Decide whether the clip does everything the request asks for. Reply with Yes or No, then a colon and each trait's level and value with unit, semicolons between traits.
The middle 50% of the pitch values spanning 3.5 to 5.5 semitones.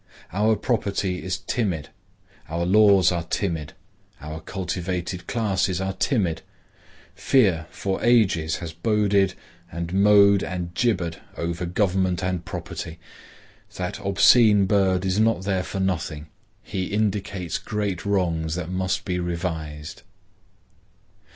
No: average, 2.8 semitones